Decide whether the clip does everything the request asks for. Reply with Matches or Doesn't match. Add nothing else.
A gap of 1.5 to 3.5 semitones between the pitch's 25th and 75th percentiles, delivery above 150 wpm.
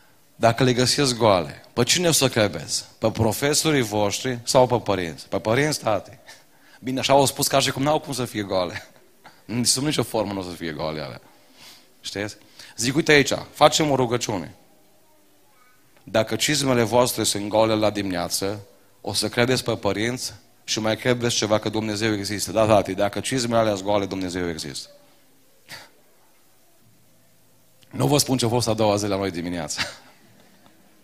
Doesn't match